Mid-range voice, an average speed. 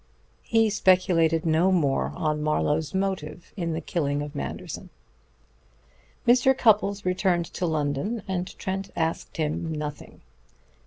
No: medium, 170 Hz; slow, 120 wpm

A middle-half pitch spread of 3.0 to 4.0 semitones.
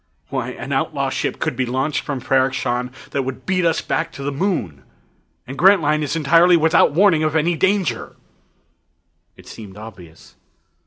No: average, 4.9 semitones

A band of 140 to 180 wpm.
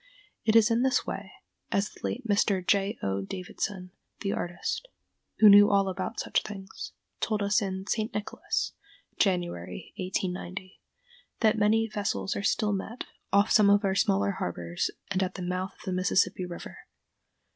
Yes: average, 160 wpm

